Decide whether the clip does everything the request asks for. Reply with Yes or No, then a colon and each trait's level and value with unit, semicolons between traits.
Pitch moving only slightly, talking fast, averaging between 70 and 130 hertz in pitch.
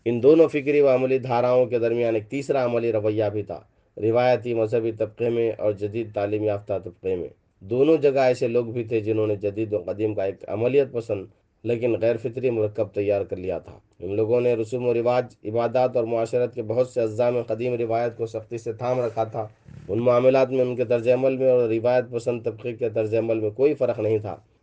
Yes: narrow, 2.2 semitones; fast, 215 wpm; low, 120 Hz